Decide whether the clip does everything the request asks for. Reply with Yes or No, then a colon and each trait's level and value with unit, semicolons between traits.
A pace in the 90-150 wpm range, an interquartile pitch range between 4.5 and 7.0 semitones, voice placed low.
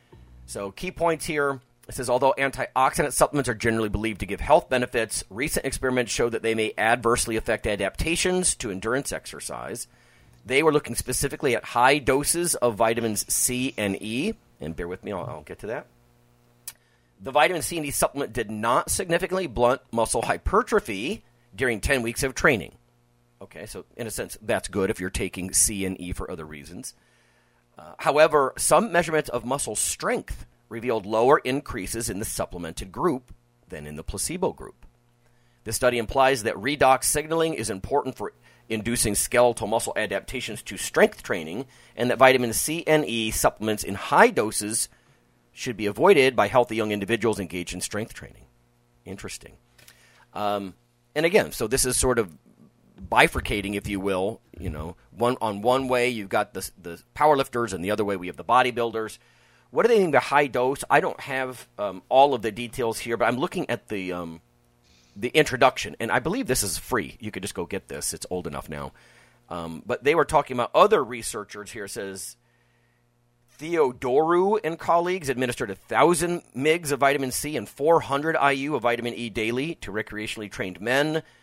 No: average, 180 wpm; average, 5.1 semitones; low, 120 Hz